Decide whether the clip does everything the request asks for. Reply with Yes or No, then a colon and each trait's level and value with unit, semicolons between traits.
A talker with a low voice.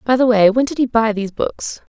No: high, 230 Hz